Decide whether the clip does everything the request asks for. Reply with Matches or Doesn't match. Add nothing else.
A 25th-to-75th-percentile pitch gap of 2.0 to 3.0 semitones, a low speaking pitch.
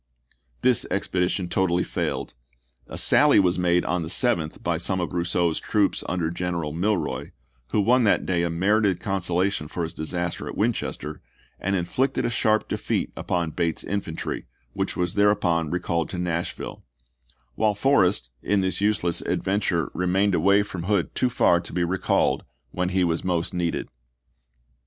Matches